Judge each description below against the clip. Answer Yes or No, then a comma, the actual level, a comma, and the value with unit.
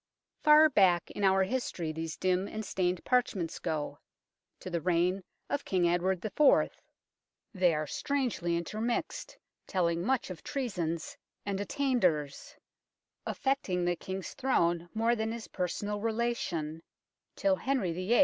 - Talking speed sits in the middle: No, slow, 130 wpm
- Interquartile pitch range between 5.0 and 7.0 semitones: Yes, wide, 5.4 semitones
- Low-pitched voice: No, high, 190 Hz